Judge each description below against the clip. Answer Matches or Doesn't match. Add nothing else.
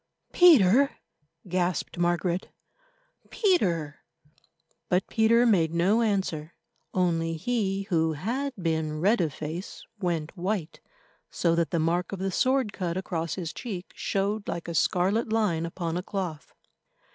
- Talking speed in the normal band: Doesn't match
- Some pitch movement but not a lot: Matches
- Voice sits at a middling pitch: Matches